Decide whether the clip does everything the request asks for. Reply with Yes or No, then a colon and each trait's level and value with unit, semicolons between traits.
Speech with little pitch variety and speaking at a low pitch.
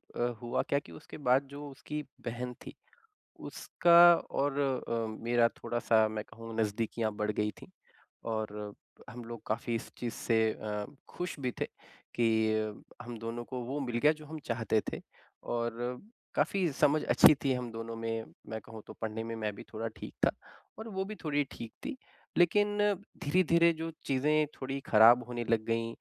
No: average, 4.2 semitones; low, 120 Hz